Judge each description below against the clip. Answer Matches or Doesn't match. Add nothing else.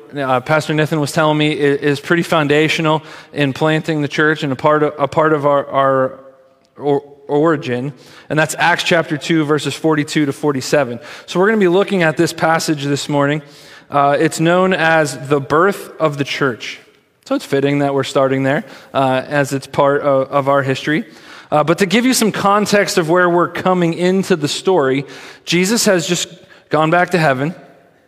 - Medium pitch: Matches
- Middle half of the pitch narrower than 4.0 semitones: Matches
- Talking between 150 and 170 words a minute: Doesn't match